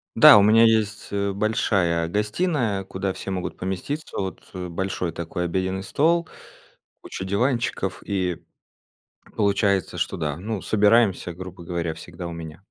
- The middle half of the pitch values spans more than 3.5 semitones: No, average, 3.2 semitones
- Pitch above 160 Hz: No, very low, 95 Hz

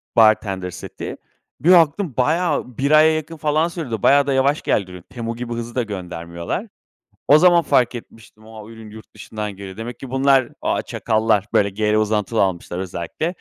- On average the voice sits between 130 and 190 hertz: No, low, 115 Hz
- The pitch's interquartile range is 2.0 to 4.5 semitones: No, wide, 5.5 semitones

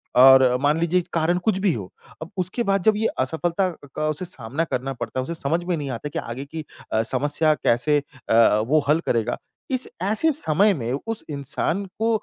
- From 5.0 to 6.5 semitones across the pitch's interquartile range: Yes, wide, 5.5 semitones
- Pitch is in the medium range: Yes, medium, 155 Hz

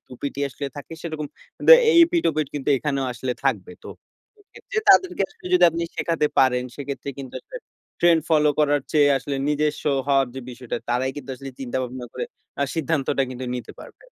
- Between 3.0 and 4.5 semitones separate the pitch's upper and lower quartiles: Yes, average, 3.5 semitones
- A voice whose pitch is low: No, medium, 145 Hz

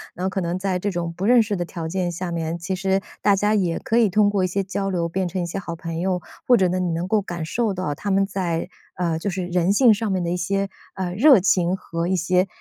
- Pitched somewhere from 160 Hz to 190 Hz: Yes, medium, 185 Hz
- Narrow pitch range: Yes, narrow, 2.3 semitones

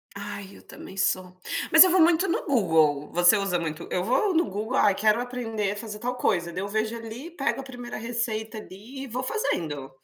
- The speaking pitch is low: No, high, 220 Hz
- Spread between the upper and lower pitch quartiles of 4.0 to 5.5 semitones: Yes, average, 5.0 semitones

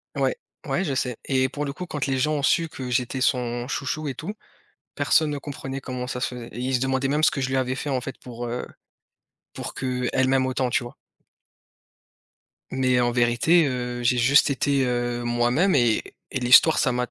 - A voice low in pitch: Yes, low, 130 Hz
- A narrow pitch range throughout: Yes, narrow, 2.2 semitones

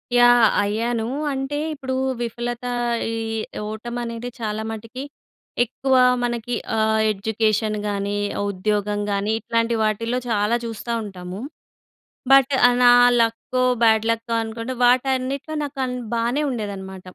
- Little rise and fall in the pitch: Yes, narrow, 2.3 semitones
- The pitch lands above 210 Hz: Yes, high, 230 Hz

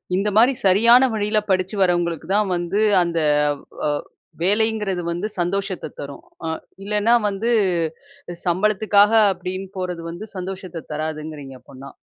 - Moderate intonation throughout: Yes, average, 3.5 semitones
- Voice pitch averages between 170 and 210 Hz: Yes, high, 190 Hz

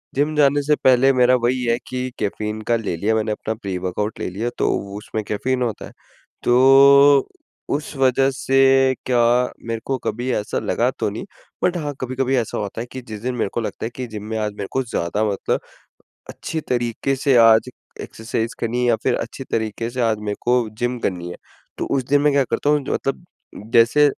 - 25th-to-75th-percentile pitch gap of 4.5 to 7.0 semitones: No, average, 3.4 semitones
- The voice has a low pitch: Yes, low, 120 Hz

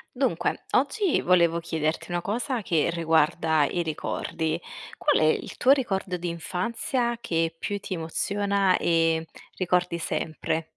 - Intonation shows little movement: No, average, 3.6 semitones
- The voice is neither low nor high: Yes, medium, 175 Hz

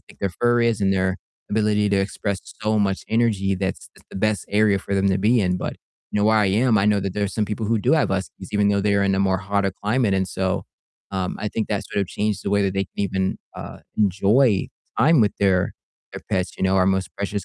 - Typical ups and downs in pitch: No, narrow, 1.7 semitones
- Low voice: Yes, low, 100 Hz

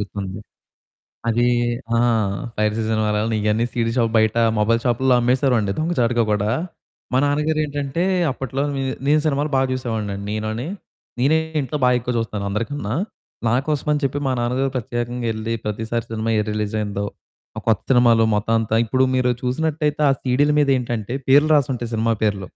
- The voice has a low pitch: Yes, low, 120 Hz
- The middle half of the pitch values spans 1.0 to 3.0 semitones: No, average, 3.6 semitones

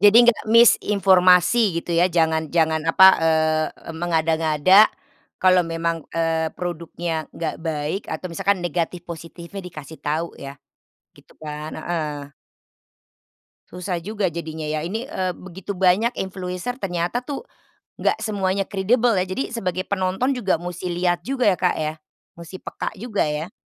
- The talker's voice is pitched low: No, medium, 175 Hz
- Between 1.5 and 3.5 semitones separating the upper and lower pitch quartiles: Yes, average, 3.2 semitones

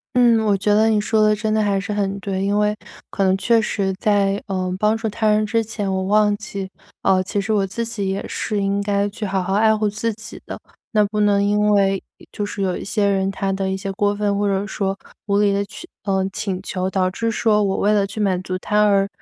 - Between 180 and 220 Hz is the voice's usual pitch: Yes, high, 205 Hz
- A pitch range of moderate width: No, narrow, 1.4 semitones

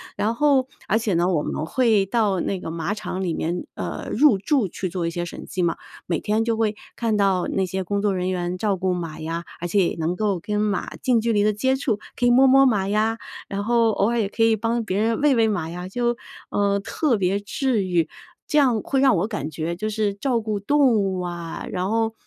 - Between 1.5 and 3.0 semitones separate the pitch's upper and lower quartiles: No, average, 4.0 semitones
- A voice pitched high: Yes, high, 205 Hz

